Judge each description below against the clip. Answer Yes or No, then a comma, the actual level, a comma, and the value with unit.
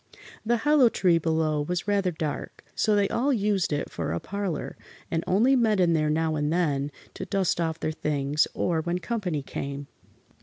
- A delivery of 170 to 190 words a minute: Yes, average, 185 wpm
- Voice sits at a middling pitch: Yes, medium, 170 Hz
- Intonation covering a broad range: No, average, 5.0 semitones